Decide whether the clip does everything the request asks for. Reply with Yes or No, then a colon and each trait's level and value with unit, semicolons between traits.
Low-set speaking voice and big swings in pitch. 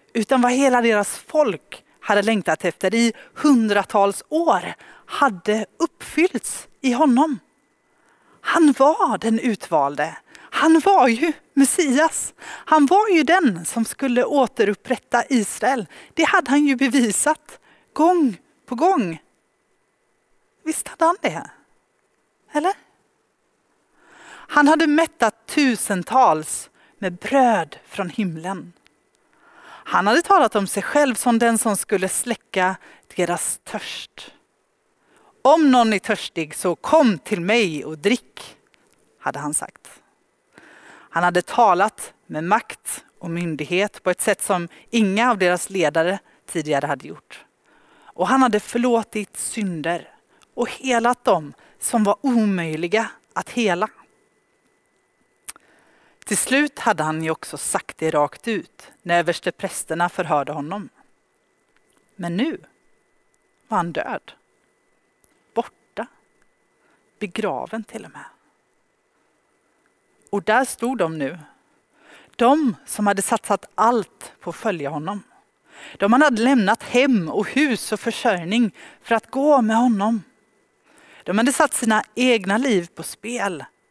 No: high, 225 Hz; wide, 5.8 semitones